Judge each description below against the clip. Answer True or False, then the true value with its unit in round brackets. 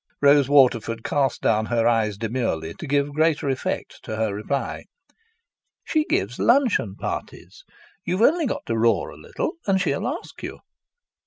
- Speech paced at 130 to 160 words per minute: True (155 wpm)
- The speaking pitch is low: True (130 Hz)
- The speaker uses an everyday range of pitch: False (6.0 semitones)